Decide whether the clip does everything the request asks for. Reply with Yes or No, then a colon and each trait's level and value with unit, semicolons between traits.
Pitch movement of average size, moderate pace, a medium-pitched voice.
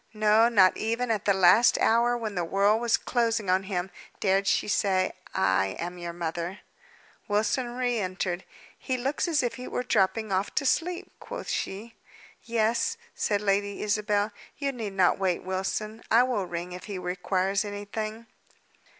No: average, 3.7 semitones; average, 165 wpm; high, 205 Hz